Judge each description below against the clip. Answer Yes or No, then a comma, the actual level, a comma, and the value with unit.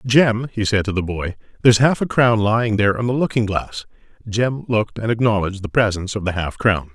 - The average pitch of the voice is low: Yes, low, 110 Hz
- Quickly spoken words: Yes, fast, 225 wpm